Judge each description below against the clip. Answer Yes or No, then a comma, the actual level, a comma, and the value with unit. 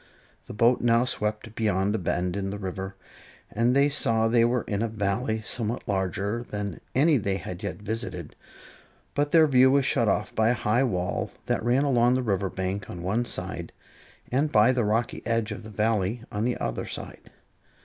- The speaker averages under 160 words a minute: No, average, 190 wpm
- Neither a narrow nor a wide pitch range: Yes, average, 3.6 semitones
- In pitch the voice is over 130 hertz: No, low, 110 Hz